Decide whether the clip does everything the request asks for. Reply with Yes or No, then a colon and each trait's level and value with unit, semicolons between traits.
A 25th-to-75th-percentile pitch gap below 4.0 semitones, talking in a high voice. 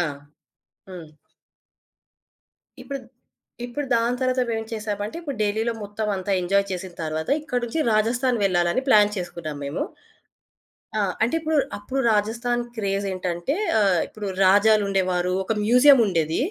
No: average, 4.5 semitones; high, 210 Hz